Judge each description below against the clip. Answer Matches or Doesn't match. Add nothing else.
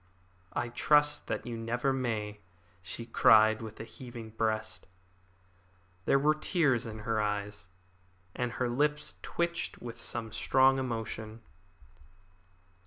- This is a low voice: Matches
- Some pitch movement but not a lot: Matches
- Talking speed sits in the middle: Doesn't match